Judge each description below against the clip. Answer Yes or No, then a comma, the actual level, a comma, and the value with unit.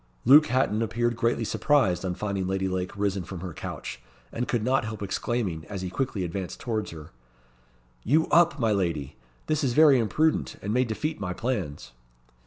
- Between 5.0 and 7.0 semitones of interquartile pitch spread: Yes, average, 5.3 semitones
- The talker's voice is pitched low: Yes, low, 110 Hz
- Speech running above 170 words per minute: Yes, average, 180 wpm